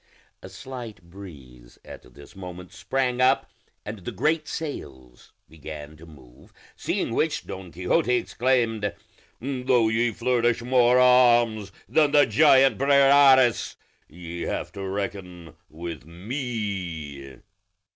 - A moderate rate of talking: No, slow, 115 wpm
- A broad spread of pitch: Yes, wide, 6.9 semitones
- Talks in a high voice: No, low, 105 Hz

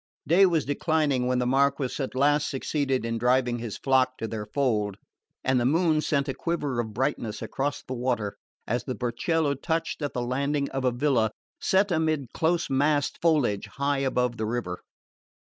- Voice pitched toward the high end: No, low, 135 Hz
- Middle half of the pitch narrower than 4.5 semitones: Yes, average, 3.3 semitones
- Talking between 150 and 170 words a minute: No, average, 180 wpm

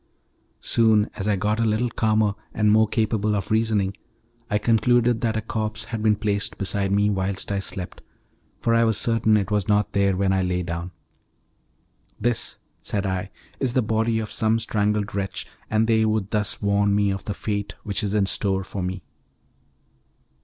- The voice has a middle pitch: No, low, 105 Hz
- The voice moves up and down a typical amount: No, narrow, 1.9 semitones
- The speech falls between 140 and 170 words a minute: No, average, 180 wpm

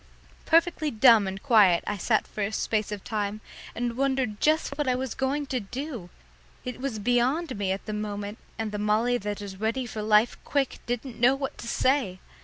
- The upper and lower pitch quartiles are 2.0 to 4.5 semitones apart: Yes, average, 4.2 semitones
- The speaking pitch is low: No, high, 230 Hz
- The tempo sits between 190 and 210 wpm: Yes, average, 200 wpm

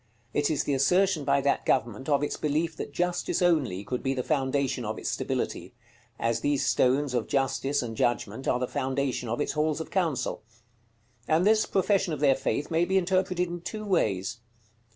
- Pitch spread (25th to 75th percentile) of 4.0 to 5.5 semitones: Yes, average, 4.8 semitones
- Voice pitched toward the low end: No, medium, 145 Hz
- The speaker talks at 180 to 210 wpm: Yes, average, 190 wpm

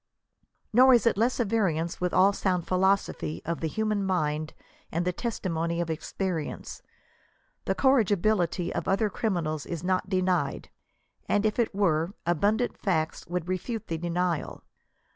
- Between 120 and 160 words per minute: Yes, average, 145 wpm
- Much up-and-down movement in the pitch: No, average, 3.7 semitones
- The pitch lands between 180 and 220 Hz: Yes, medium, 185 Hz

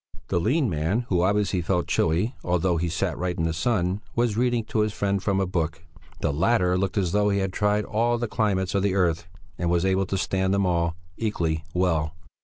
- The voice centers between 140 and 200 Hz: No, very low, 95 Hz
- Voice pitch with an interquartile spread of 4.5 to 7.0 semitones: No, average, 3.3 semitones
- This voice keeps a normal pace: No, fast, 215 wpm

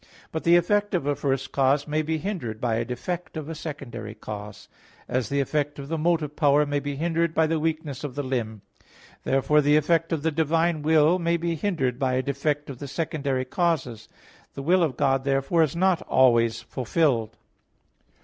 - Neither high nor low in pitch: Yes, medium, 145 Hz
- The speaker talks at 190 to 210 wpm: Yes, average, 195 wpm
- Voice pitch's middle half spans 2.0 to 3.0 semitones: No, average, 3.7 semitones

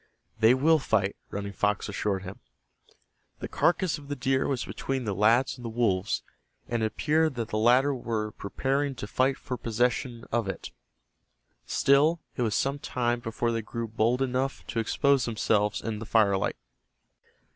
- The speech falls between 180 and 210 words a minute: No, average, 165 wpm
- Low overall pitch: Yes, low, 120 Hz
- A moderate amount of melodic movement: Yes, average, 3.7 semitones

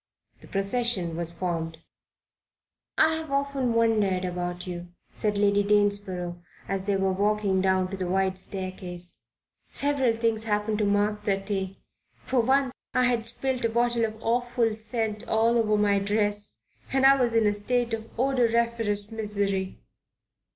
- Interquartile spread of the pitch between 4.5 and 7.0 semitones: No, average, 3.3 semitones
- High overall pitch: Yes, high, 210 Hz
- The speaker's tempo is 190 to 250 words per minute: No, average, 145 wpm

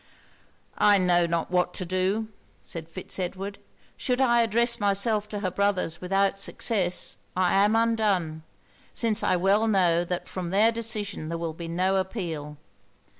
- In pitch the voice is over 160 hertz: Yes, high, 190 Hz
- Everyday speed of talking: Yes, average, 155 wpm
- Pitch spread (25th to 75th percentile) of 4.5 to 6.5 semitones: No, average, 3.3 semitones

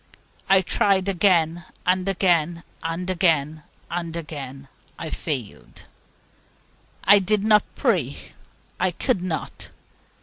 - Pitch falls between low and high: Yes, medium, 175 Hz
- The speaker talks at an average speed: No, slow, 105 wpm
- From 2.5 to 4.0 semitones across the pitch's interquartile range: Yes, average, 3.0 semitones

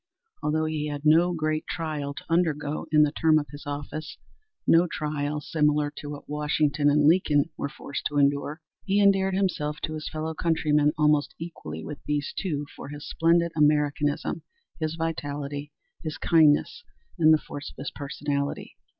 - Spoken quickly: No, average, 165 wpm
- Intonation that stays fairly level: Yes, narrow, 1.7 semitones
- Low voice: No, medium, 150 Hz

